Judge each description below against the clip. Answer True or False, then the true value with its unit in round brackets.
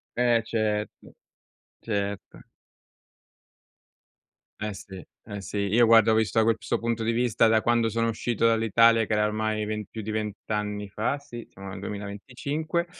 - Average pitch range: False (1.9 semitones)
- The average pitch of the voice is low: True (110 Hz)